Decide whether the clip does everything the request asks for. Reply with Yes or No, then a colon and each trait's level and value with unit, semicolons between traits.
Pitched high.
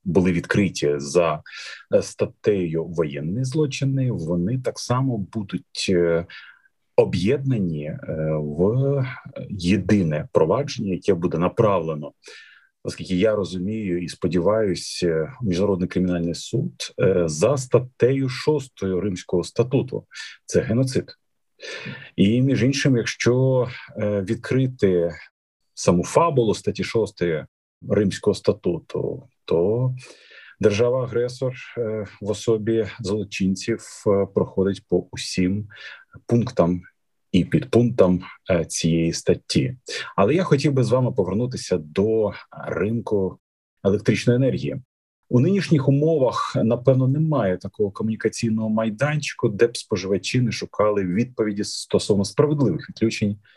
No: low, 110 Hz